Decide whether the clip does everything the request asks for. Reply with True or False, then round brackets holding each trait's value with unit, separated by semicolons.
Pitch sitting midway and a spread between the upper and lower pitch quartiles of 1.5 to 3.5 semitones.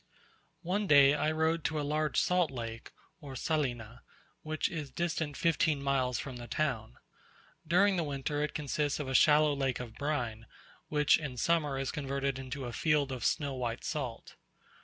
True (145 Hz; 3.0 semitones)